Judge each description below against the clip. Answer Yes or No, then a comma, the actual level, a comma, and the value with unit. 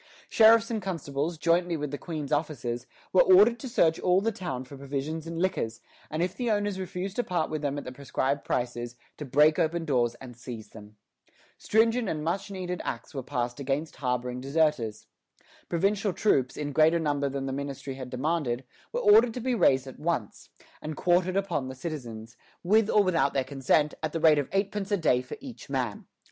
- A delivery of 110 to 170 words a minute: No, average, 195 wpm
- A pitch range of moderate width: No, wide, 5.8 semitones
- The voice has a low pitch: No, medium, 155 Hz